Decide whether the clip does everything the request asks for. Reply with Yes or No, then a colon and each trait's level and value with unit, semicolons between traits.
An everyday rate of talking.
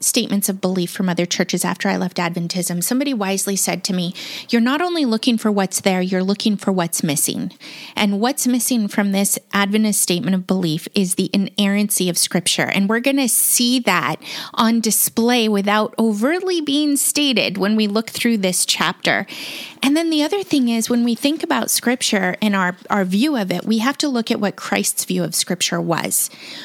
Yes: average, 195 wpm